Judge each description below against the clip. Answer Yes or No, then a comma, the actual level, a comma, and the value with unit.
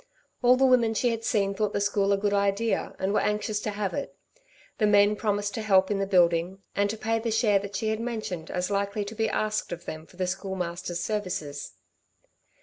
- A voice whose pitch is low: No, high, 205 Hz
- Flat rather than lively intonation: Yes, narrow, 2.3 semitones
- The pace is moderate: No, fast, 225 wpm